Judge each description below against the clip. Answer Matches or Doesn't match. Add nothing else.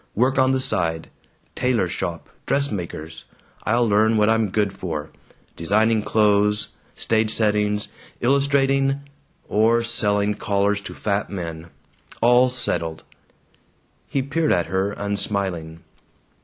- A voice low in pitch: Matches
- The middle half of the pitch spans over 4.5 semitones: Doesn't match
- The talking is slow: Matches